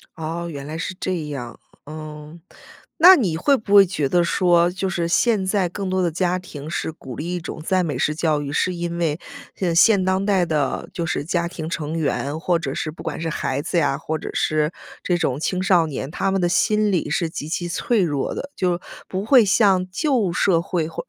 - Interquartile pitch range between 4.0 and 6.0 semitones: No, average, 3.2 semitones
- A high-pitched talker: No, medium, 170 Hz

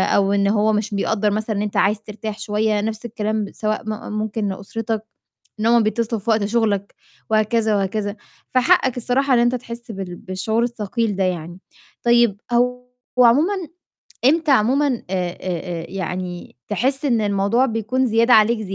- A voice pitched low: No, high, 215 Hz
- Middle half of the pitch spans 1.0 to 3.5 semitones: Yes, average, 2.8 semitones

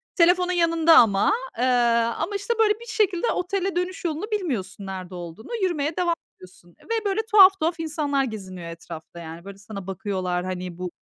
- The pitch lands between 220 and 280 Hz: No, very high, 295 Hz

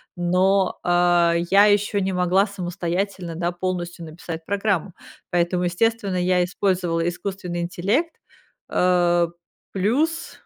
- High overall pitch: No, medium, 180 Hz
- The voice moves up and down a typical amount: No, narrow, 2.3 semitones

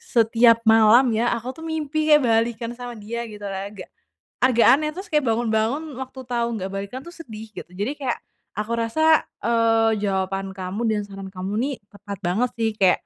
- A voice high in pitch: Yes, high, 225 Hz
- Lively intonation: No, average, 3.2 semitones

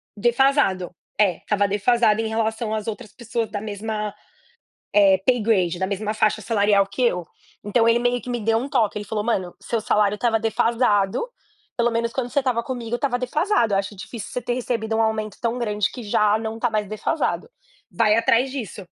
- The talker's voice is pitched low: No, high, 220 Hz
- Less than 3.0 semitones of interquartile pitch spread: Yes, narrow, 2.4 semitones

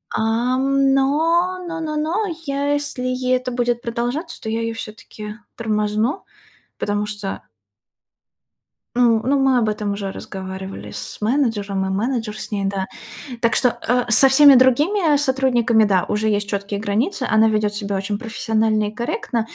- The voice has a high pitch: Yes, high, 230 Hz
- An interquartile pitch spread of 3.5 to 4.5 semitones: Yes, average, 4.2 semitones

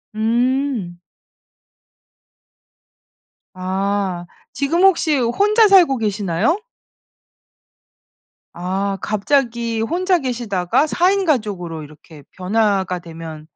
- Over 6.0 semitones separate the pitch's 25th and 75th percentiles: Yes, wide, 7.4 semitones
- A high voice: Yes, high, 220 Hz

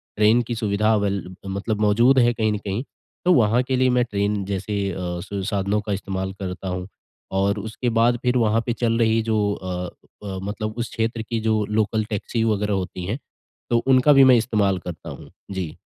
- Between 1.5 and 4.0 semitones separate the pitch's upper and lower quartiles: Yes, average, 2.8 semitones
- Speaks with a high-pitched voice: No, low, 105 Hz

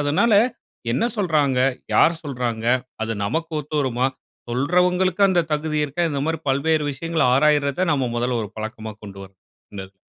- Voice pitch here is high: No, medium, 145 Hz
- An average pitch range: Yes, average, 5.0 semitones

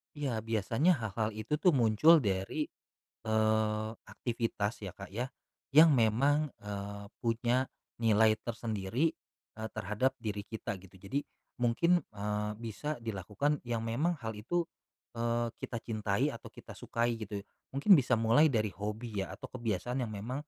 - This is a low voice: Yes, low, 115 Hz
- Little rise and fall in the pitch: No, average, 3.5 semitones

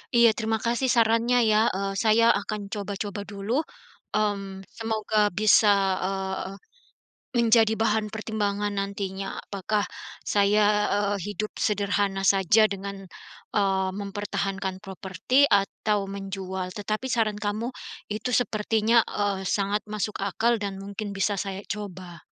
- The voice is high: Yes, high, 205 Hz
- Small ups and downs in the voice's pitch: Yes, narrow, 1.8 semitones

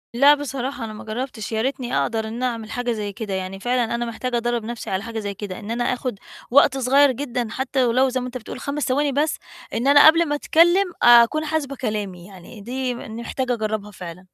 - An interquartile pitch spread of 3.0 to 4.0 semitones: Yes, average, 3.5 semitones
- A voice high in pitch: Yes, high, 240 Hz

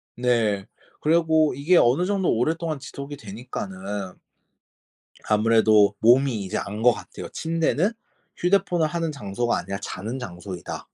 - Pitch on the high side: No, low, 125 Hz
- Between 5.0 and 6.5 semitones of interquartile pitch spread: No, wide, 7.4 semitones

